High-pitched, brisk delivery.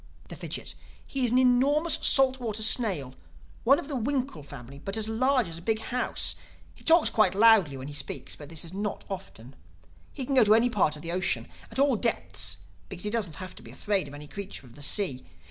Yes: high, 210 Hz; fast, 220 wpm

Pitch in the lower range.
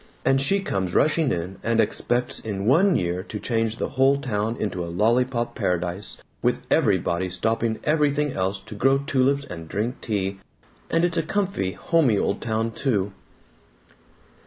Yes: low, 115 Hz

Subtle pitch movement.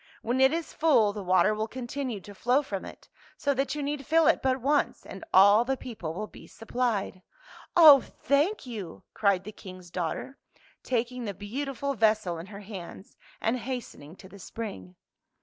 No: wide, 5.4 semitones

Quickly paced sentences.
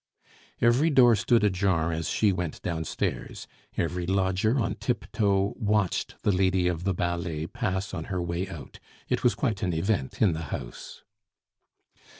No: average, 155 wpm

